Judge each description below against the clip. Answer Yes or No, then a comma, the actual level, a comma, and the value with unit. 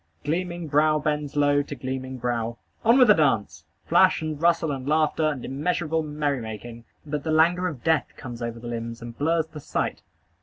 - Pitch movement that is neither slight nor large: Yes, average, 4.2 semitones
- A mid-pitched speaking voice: Yes, medium, 150 Hz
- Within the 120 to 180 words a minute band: No, average, 190 wpm